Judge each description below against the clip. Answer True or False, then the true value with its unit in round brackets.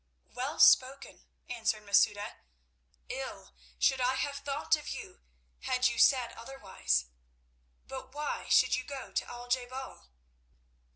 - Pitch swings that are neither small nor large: True (3.3 semitones)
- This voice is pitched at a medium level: False (255 Hz)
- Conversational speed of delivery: False (130 wpm)